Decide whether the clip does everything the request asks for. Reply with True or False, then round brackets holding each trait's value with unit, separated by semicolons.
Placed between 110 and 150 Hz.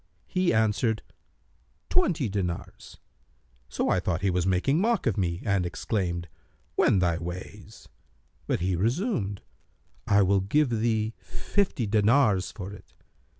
False (100 Hz)